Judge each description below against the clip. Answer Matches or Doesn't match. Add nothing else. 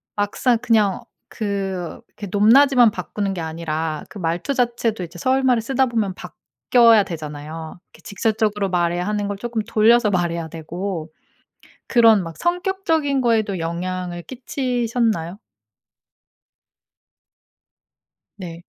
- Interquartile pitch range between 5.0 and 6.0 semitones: Matches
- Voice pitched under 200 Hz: Doesn't match